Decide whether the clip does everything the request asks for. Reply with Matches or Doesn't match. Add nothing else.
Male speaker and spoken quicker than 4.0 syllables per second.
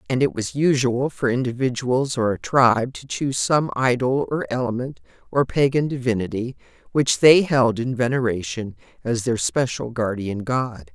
Doesn't match